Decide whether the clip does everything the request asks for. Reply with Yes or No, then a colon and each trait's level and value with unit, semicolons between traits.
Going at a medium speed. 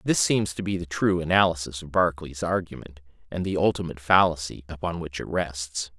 Yes: average, 180 wpm